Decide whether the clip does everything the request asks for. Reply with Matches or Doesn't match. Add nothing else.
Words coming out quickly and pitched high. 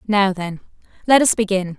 Doesn't match